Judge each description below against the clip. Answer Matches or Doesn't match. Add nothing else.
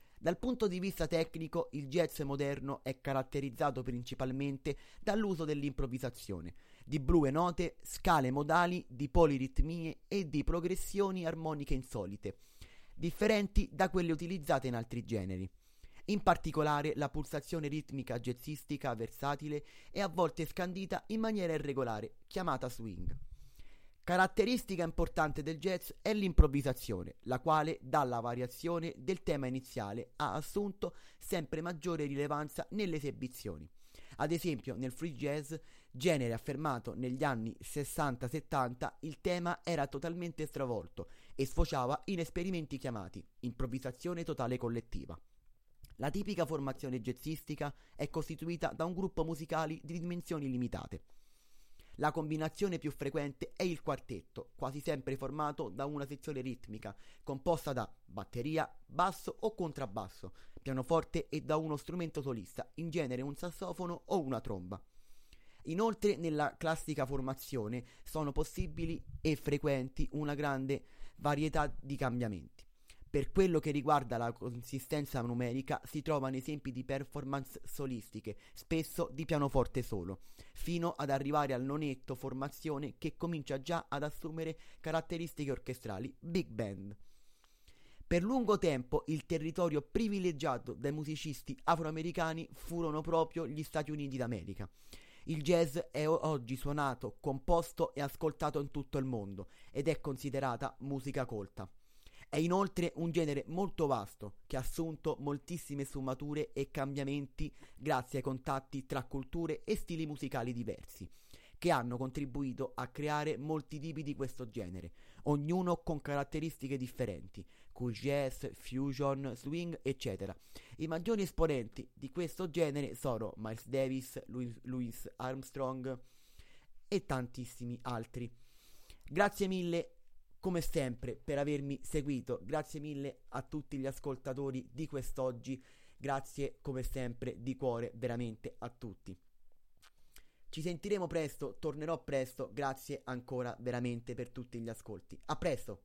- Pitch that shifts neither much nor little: Matches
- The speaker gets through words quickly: Doesn't match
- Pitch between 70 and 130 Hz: Doesn't match